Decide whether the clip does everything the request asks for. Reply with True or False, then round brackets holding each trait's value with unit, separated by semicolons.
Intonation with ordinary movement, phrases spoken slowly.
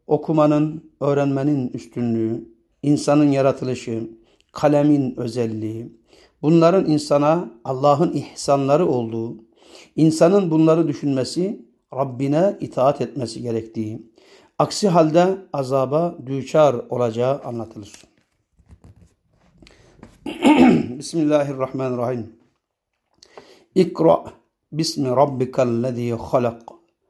True (4.1 semitones; 65 wpm)